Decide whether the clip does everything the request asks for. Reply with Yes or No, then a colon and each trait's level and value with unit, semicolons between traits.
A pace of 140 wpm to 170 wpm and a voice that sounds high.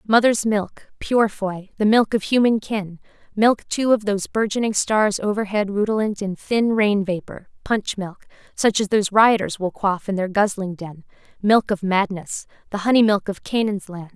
Yes: average, 165 wpm; high, 205 Hz